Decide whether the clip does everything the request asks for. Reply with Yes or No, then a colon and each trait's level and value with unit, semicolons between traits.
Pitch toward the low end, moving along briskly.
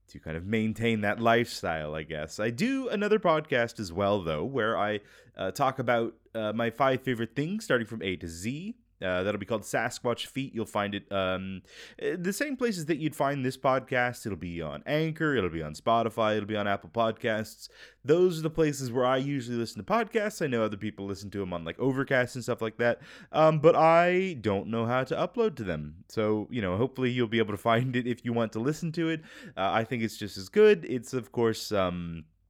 Yes: low, 115 Hz; fast, 225 wpm